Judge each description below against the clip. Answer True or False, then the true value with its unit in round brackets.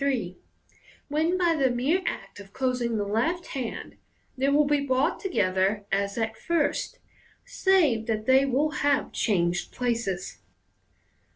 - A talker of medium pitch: False (255 Hz)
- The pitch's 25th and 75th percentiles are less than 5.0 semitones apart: False (5.4 semitones)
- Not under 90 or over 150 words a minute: True (135 wpm)